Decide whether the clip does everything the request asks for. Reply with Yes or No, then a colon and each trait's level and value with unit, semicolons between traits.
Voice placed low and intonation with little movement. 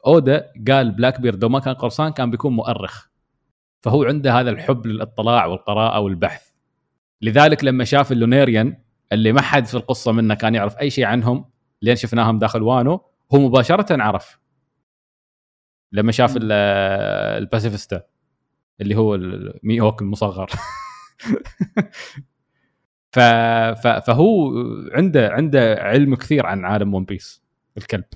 No: low, 120 Hz; average, 4.1 semitones